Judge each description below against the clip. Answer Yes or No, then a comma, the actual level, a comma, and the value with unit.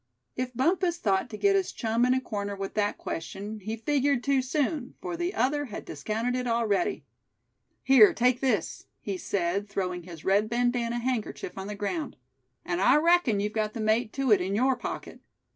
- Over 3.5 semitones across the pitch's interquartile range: Yes, average, 4.5 semitones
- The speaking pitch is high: Yes, high, 230 Hz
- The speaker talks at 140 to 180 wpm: No, average, 190 wpm